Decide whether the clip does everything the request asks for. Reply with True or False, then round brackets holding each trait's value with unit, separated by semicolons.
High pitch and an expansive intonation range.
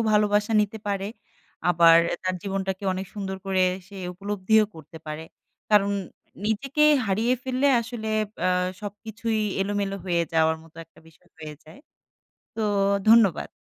False (200 Hz; 3.5 semitones)